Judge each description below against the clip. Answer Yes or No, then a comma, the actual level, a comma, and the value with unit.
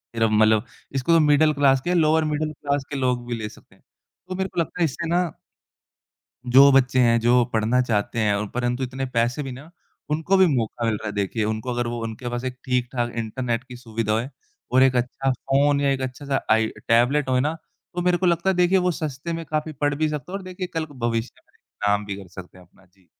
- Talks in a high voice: No, low, 130 Hz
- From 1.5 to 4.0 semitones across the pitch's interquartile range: No, average, 4.7 semitones